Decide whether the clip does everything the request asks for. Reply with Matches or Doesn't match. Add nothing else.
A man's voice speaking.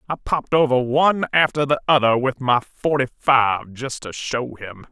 Matches